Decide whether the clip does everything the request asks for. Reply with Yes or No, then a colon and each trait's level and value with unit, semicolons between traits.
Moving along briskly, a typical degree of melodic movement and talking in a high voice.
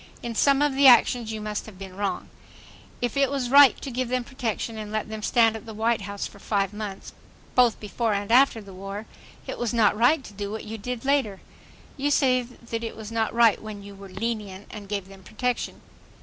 Yes: fast, 220 wpm; average, 3.3 semitones; high, 220 Hz